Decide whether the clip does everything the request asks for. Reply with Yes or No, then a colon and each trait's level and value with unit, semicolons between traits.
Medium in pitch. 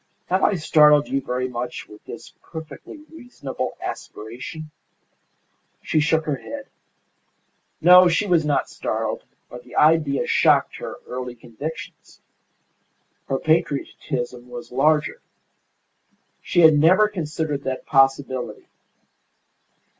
Yes: medium, 150 Hz